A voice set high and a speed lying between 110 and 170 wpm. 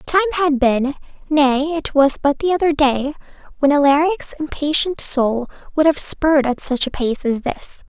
Yes: very high, 290 Hz; average, 160 wpm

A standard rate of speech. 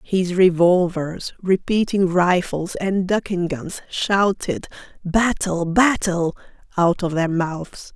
No: slow, 105 wpm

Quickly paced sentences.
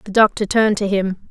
Yes: fast, 230 wpm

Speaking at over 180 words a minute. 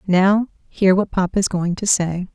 Yes: fast, 205 wpm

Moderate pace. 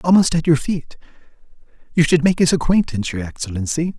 Yes: average, 165 wpm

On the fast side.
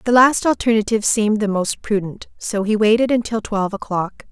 No: average, 180 wpm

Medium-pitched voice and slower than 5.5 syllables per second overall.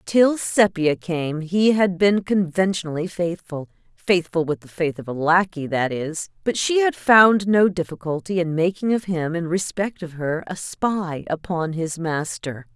Yes: medium, 175 Hz; 4.2 syllables/s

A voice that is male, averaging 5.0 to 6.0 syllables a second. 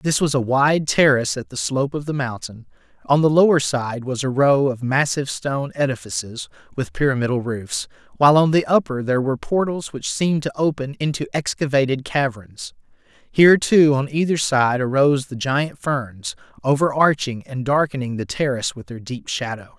Yes: male; 5.3 syllables/s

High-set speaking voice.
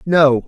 No: medium, 145 Hz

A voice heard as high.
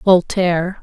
No: medium, 180 Hz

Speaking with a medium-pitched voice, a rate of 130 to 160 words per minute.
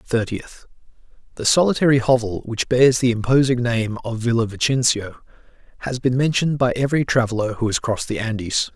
No: low, 120 Hz; average, 150 wpm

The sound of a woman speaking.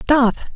Yes: female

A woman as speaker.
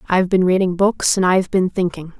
Yes: female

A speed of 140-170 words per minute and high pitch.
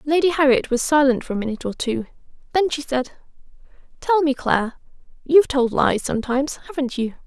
Yes: average, 165 wpm; very high, 270 Hz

